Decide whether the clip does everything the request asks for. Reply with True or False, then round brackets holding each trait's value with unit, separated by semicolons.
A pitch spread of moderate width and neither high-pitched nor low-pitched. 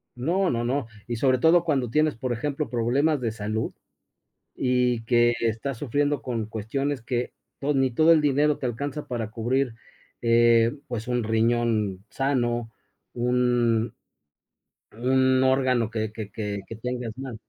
False (3.0 semitones; 120 Hz)